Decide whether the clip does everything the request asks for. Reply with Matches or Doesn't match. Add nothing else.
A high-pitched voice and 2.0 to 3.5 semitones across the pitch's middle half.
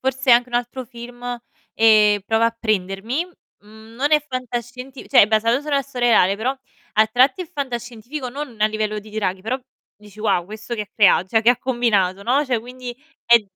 Matches